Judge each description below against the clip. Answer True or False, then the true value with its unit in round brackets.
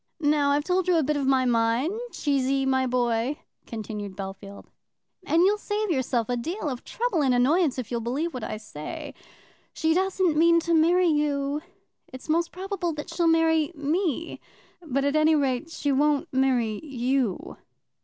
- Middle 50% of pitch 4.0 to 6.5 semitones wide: True (4.7 semitones)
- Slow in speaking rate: False (170 wpm)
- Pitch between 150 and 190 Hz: False (290 Hz)